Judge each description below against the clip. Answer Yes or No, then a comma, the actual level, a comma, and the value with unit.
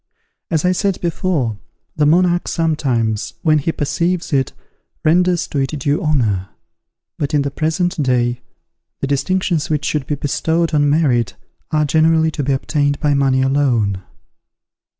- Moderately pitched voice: Yes, medium, 150 Hz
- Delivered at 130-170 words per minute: Yes, average, 150 wpm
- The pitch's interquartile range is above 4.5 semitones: No, average, 3.4 semitones